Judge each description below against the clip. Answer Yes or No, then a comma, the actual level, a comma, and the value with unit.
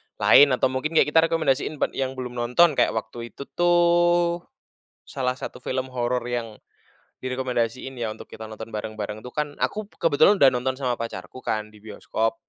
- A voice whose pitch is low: Yes, low, 130 Hz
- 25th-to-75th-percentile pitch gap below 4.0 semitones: No, average, 4.4 semitones